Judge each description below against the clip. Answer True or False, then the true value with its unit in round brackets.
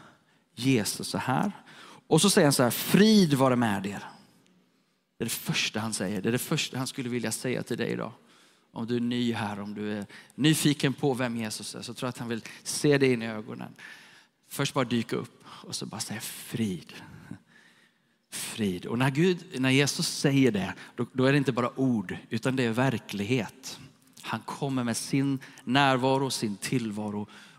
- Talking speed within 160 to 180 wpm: False (190 wpm)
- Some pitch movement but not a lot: True (3.4 semitones)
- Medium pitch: False (130 Hz)